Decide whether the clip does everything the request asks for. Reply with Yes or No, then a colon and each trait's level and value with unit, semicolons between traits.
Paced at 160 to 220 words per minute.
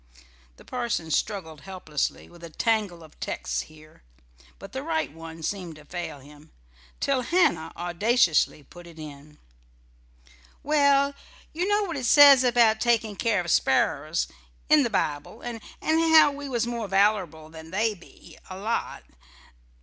No: average, 150 wpm